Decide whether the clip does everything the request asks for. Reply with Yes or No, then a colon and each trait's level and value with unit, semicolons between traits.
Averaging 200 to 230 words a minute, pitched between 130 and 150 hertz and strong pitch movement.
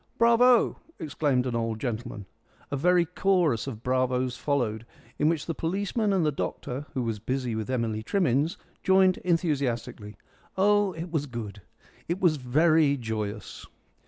No: average, 145 wpm; medium, 140 Hz; wide, 6.6 semitones